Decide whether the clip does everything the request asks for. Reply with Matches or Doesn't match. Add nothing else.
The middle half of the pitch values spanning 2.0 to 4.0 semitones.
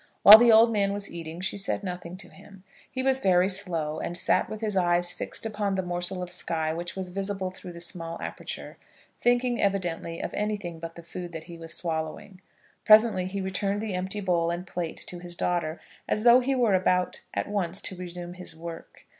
Matches